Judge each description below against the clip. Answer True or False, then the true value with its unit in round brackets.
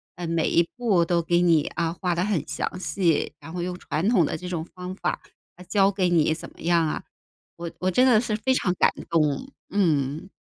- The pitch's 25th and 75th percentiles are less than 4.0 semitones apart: True (2.7 semitones)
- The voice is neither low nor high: True (175 Hz)